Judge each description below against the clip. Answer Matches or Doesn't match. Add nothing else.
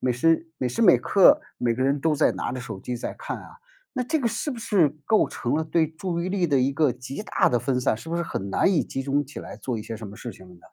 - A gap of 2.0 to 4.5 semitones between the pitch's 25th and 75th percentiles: Doesn't match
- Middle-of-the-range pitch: Matches